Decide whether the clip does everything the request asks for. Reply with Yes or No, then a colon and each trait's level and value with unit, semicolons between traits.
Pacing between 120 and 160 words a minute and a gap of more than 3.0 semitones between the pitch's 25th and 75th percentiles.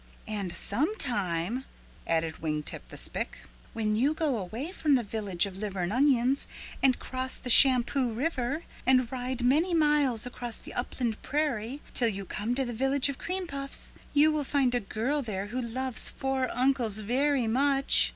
No: average, 170 wpm; average, 4.2 semitones